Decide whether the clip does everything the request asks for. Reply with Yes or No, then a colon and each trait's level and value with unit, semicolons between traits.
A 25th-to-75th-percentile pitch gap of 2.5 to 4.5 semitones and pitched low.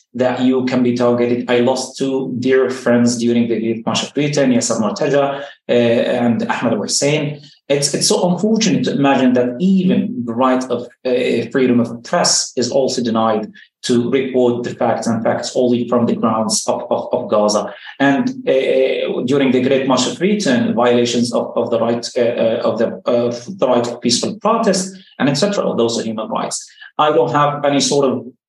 Yes: average, 3.3 semitones; low, 130 Hz